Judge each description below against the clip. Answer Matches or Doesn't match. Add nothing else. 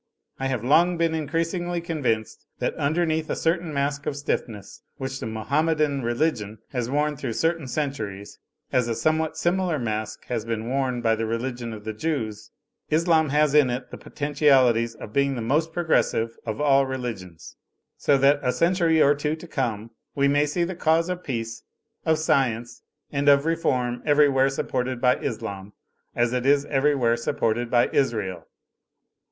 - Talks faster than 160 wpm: Matches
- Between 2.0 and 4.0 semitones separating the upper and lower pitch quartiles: Doesn't match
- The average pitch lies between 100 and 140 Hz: Matches